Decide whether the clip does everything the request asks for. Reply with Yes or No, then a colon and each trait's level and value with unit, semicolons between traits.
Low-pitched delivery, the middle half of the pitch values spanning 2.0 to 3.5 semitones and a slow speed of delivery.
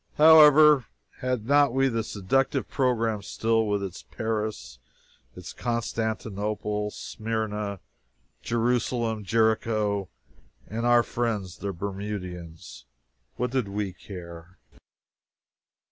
Yes: low, 110 Hz; average, 3.1 semitones; slow, 95 wpm